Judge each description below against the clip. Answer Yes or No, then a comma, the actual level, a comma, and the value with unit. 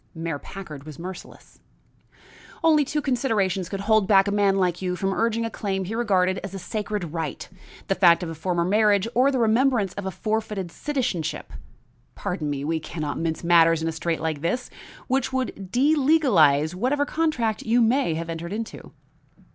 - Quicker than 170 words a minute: Yes, average, 180 wpm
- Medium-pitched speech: No, high, 195 Hz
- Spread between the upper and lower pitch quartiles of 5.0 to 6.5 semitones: Yes, average, 5.3 semitones